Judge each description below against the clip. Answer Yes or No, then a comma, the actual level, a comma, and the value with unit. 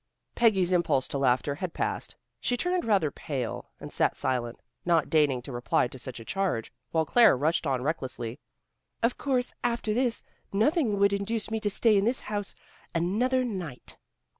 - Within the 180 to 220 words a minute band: No, average, 170 wpm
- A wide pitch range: Yes, wide, 8.6 semitones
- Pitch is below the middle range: No, medium, 185 Hz